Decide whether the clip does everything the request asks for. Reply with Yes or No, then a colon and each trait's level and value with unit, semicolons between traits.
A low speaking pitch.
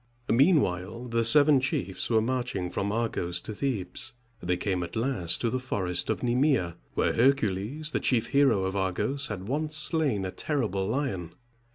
Yes: low, 115 Hz